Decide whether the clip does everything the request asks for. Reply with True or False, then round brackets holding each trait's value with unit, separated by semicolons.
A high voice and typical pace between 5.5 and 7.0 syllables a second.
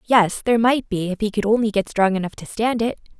True (215 Hz; 6.0 syllables/s)